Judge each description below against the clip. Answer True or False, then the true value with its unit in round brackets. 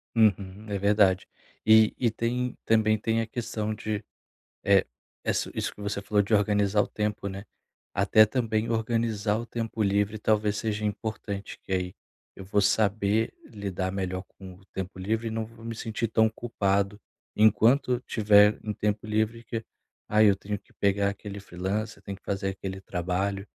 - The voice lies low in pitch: True (105 Hz)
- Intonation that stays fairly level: True (1.9 semitones)